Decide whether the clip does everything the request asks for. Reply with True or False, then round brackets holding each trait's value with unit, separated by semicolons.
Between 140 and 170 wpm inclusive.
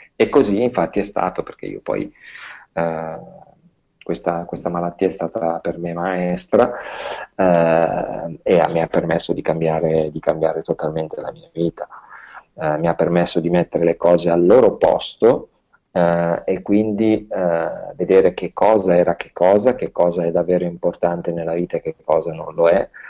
True (165 wpm)